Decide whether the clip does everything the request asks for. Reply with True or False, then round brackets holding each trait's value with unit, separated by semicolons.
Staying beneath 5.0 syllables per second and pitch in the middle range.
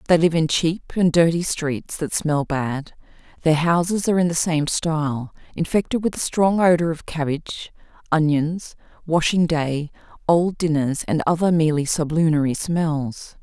True (4.6 syllables/s; 160 Hz)